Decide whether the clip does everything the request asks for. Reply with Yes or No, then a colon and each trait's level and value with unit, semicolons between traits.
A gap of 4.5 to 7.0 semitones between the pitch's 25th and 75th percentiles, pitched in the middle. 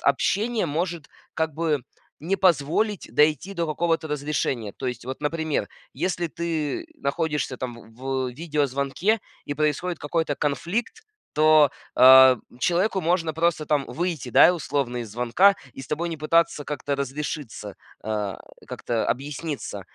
No: average, 4.1 semitones; medium, 150 Hz